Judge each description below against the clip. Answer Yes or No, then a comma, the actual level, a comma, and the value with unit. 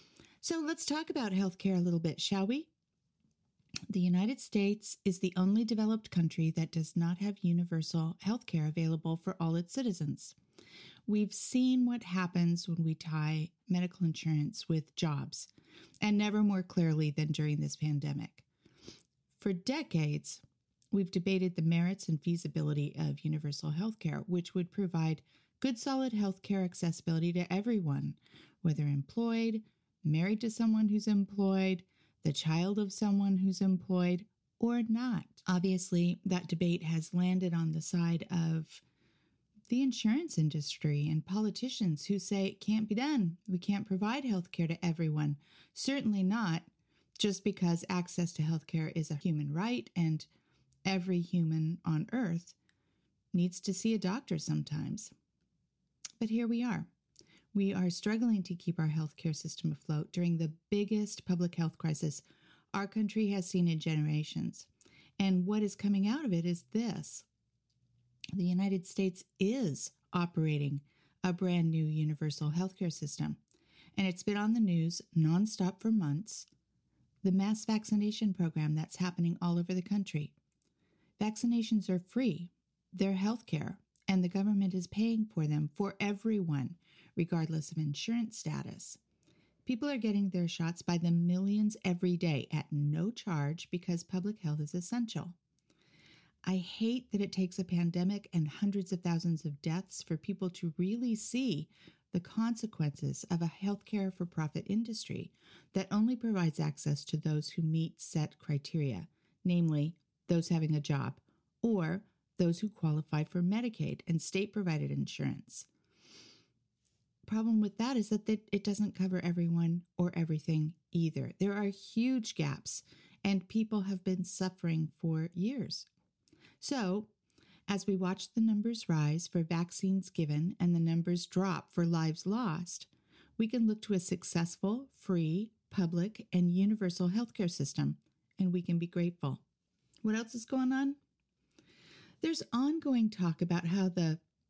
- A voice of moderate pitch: Yes, medium, 180 Hz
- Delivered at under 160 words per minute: Yes, average, 145 wpm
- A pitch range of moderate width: Yes, average, 4.1 semitones